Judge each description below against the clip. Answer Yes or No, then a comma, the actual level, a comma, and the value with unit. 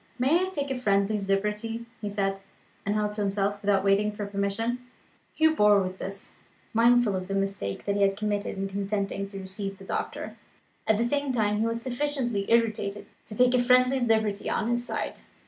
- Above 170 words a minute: Yes, average, 190 wpm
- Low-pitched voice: No, high, 210 Hz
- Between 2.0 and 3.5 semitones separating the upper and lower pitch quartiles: Yes, average, 3.2 semitones